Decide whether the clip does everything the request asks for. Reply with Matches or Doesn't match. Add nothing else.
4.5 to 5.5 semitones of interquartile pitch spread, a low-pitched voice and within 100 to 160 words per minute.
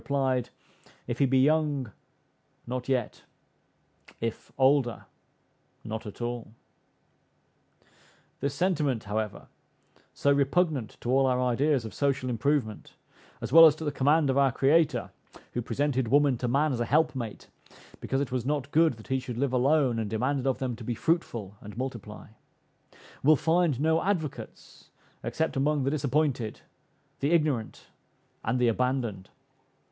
Doesn't match